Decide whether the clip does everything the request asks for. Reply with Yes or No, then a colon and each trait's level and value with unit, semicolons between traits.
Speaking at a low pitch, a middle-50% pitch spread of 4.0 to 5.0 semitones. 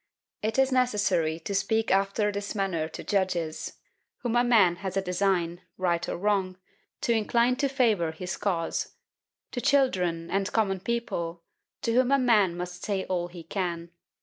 No: high, 195 Hz; average, 4.3 semitones